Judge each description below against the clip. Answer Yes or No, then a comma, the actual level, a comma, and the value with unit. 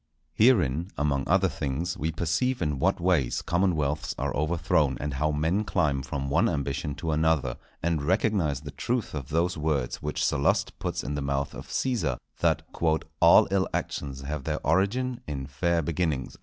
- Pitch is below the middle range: Yes, very low, 75 Hz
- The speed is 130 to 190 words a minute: Yes, average, 170 wpm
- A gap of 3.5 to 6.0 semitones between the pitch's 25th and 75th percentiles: Yes, average, 3.8 semitones